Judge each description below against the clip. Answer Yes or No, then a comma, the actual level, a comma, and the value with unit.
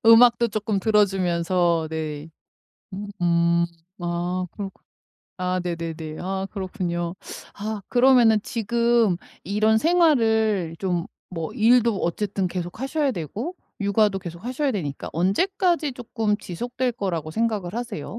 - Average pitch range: Yes, average, 5.0 semitones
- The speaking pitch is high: Yes, high, 200 Hz